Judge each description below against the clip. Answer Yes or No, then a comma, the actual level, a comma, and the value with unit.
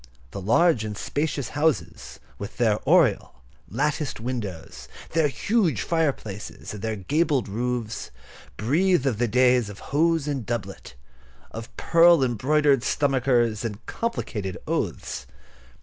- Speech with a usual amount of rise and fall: No, wide, 5.7 semitones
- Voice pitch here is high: No, low, 125 Hz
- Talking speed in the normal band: No, slow, 120 wpm